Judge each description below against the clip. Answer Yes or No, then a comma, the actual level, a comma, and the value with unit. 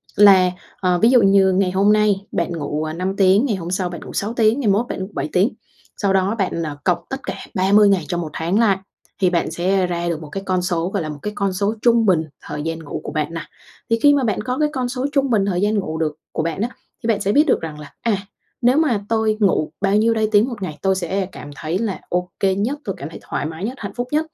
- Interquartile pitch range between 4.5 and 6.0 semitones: No, average, 4.0 semitones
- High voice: Yes, high, 195 Hz